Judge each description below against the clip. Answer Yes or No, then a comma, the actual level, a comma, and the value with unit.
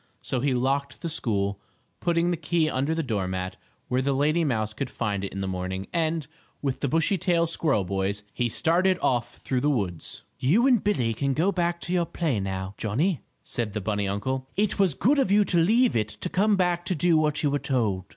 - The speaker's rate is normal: No, fast, 215 wpm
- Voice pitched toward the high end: No, medium, 140 Hz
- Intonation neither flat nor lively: No, wide, 8.2 semitones